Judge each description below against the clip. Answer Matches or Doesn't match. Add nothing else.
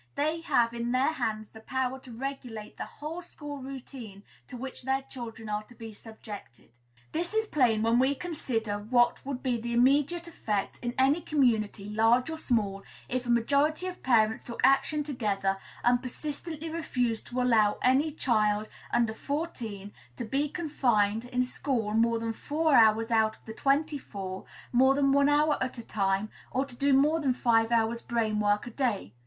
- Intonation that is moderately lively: Matches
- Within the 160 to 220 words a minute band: Matches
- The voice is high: Matches